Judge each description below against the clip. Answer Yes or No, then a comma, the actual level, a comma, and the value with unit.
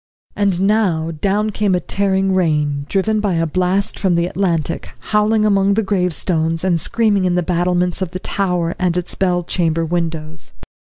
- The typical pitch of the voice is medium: Yes, medium, 180 Hz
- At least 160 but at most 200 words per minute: Yes, average, 170 wpm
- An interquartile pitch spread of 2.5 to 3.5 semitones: Yes, average, 3.0 semitones